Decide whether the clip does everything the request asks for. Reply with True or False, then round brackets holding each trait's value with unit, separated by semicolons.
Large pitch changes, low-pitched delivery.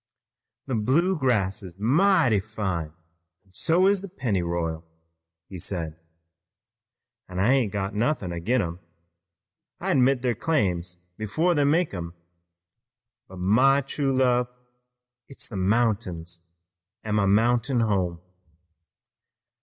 True (6.5 semitones; 110 Hz)